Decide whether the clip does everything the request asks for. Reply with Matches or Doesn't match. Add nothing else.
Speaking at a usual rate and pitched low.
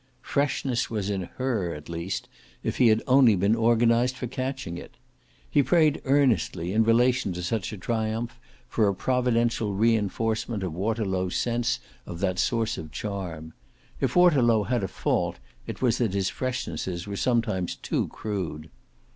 Matches